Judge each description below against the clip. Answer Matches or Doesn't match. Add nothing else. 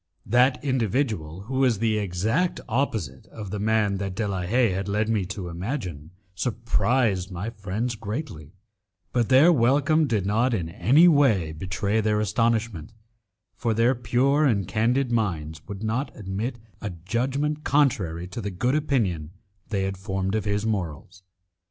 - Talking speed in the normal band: Matches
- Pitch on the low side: Matches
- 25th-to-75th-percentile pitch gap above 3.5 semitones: Matches